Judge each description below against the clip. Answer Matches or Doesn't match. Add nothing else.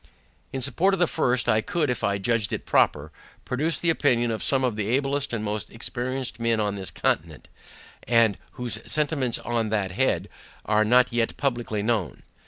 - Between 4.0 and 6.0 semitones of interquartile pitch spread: Doesn't match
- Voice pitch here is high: Doesn't match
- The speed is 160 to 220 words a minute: Matches